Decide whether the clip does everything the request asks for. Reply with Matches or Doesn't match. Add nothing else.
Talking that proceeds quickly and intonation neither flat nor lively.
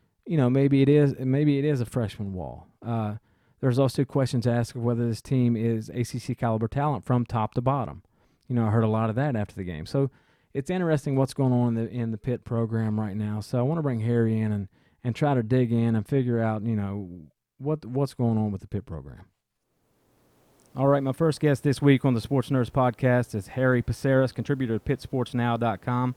Matches